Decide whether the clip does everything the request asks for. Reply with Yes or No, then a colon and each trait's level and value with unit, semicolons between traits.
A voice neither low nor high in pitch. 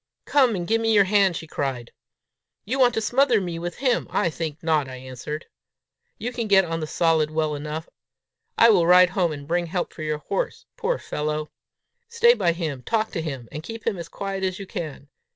Yes: medium, 175 Hz